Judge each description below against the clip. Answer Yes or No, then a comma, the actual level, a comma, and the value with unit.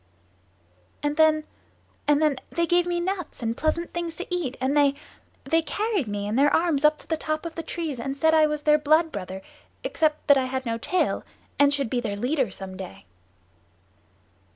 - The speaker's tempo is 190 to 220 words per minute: Yes, average, 200 wpm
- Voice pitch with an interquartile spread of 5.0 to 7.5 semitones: No, average, 4.0 semitones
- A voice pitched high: Yes, very high, 295 Hz